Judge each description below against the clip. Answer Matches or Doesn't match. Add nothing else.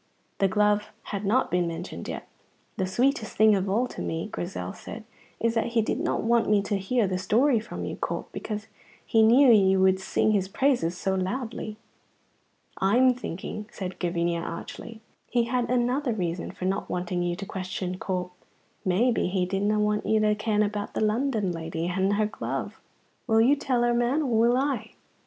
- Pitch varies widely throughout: Doesn't match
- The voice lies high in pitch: Matches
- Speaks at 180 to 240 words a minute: Matches